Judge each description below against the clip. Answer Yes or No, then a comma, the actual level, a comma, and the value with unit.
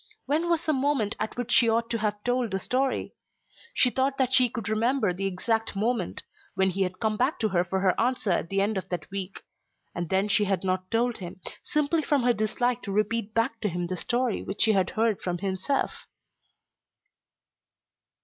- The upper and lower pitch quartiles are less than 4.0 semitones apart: No, average, 4.4 semitones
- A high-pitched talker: Yes, high, 220 Hz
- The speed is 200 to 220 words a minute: Yes, fast, 205 wpm